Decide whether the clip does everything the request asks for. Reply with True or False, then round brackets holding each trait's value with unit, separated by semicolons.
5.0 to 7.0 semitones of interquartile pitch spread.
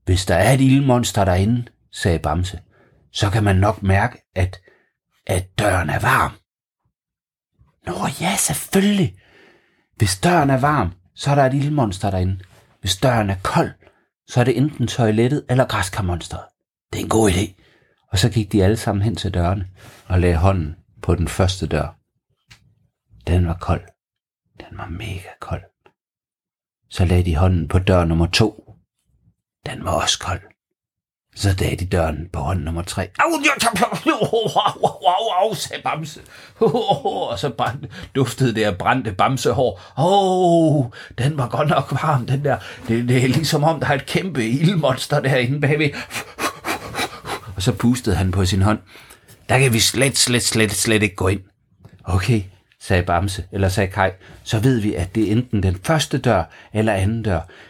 True (5.4 semitones)